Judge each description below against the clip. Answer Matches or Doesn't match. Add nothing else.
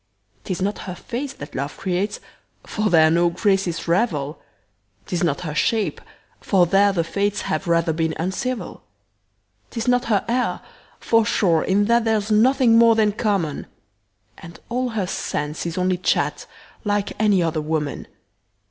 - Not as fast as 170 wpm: Matches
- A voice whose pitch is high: Matches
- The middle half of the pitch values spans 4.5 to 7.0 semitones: Matches